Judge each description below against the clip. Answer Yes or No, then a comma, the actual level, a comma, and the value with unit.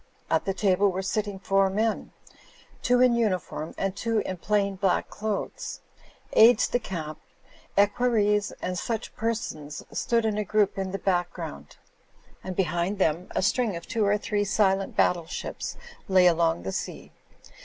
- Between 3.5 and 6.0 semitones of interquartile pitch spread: No, average, 2.9 semitones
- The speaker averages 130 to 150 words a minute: No, average, 165 wpm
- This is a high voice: Yes, high, 195 Hz